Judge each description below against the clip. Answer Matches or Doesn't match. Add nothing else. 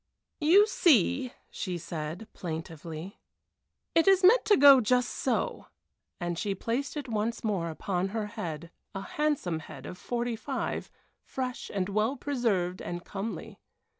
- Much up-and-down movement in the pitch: Matches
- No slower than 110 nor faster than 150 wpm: Matches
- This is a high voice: Matches